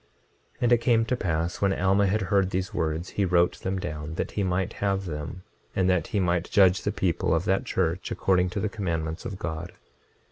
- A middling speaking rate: No, fast, 215 wpm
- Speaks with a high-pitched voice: No, very low, 95 Hz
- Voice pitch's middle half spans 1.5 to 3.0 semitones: Yes, narrow, 2.6 semitones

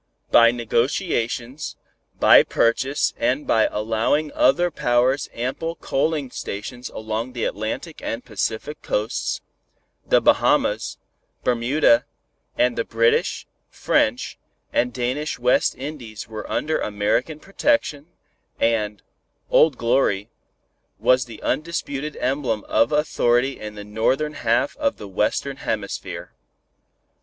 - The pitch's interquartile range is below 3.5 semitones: No, average, 4.4 semitones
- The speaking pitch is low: Yes, low, 125 Hz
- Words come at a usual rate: No, slow, 110 wpm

